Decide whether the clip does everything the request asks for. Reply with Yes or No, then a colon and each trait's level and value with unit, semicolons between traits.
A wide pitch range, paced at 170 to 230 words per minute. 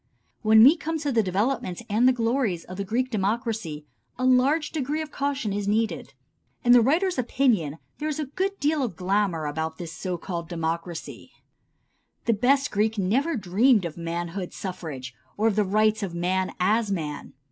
Yes: wide, 6.3 semitones; average, 175 wpm